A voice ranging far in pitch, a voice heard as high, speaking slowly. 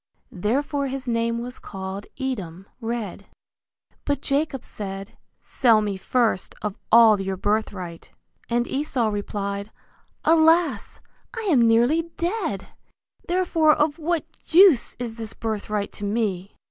Yes: wide, 6.0 semitones; high, 230 Hz; slow, 120 wpm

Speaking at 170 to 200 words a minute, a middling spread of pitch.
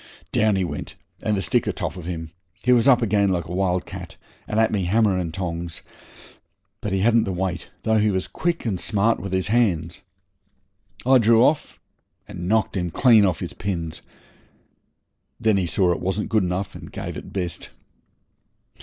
Yes: average, 185 wpm; average, 3.7 semitones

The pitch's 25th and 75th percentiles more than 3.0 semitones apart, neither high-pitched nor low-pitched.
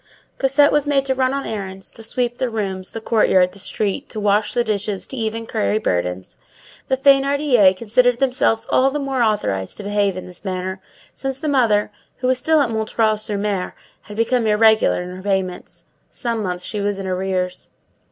No: average, 4.7 semitones; high, 215 Hz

